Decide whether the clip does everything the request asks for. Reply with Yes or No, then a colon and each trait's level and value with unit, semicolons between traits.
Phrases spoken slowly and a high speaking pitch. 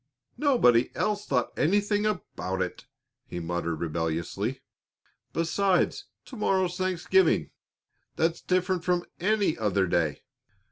No: slow, 105 wpm; medium, 170 Hz